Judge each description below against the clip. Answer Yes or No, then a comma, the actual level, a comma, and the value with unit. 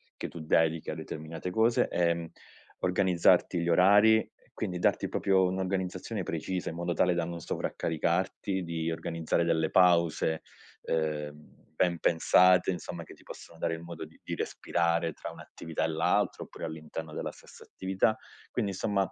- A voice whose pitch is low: Yes, very low, 85 Hz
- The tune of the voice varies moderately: No, narrow, 2.2 semitones